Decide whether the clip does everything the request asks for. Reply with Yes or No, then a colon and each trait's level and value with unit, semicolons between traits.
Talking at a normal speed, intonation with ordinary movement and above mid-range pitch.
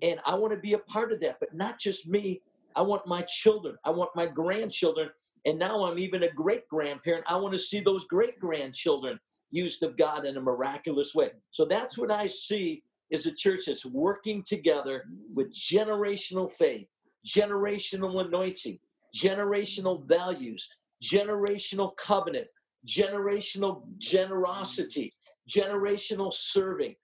Yes: average, 145 wpm; average, 3.2 semitones; high, 200 Hz